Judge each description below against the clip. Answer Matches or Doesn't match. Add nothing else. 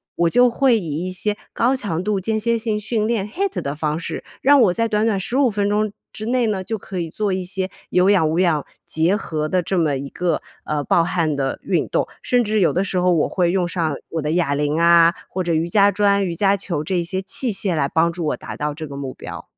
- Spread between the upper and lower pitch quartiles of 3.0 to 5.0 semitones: Matches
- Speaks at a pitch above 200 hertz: Doesn't match